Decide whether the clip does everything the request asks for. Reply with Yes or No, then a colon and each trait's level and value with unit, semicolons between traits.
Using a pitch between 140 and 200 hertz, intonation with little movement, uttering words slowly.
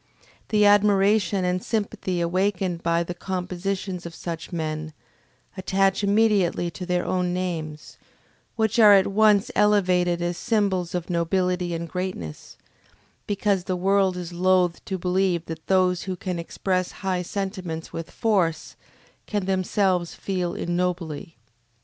Yes: medium, 185 Hz; narrow, 2.2 semitones; slow, 130 wpm